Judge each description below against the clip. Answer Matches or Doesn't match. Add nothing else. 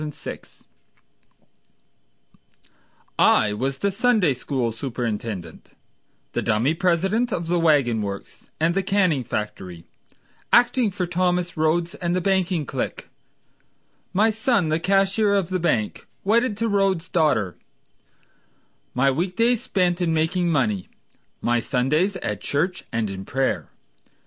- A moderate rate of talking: Doesn't match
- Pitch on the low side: Doesn't match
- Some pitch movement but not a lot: Doesn't match